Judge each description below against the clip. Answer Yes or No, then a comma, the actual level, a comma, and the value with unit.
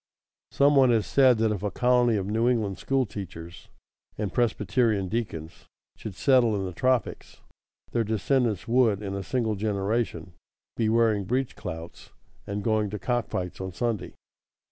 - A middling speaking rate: Yes, average, 160 wpm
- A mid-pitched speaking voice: No, low, 110 Hz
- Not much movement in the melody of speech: No, average, 3.7 semitones